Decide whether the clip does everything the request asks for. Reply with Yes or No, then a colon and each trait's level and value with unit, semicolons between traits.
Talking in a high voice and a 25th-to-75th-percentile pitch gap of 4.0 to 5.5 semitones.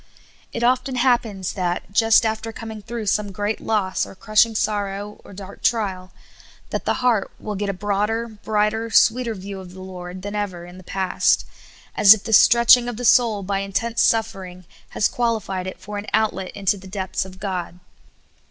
No: high, 205 Hz; average, 2.9 semitones